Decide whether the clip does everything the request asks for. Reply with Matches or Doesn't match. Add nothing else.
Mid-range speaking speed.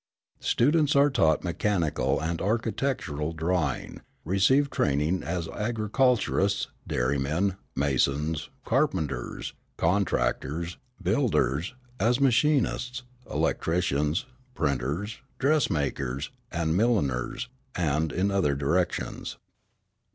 Doesn't match